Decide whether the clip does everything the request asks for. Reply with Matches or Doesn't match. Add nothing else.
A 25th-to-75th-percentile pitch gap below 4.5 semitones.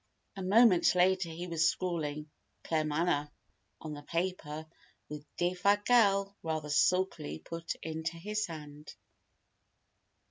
Matches